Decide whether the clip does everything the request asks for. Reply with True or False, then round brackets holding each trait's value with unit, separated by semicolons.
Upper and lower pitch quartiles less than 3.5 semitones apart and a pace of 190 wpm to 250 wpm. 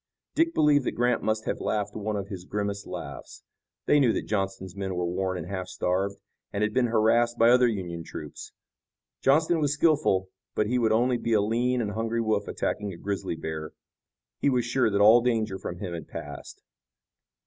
False (4.0 semitones; 195 wpm)